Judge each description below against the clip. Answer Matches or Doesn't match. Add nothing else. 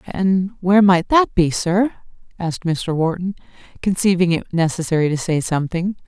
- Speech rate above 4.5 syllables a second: Matches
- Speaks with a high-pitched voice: Doesn't match